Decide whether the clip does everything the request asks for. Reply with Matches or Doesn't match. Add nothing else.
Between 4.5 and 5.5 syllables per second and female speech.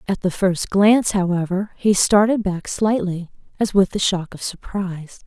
Matches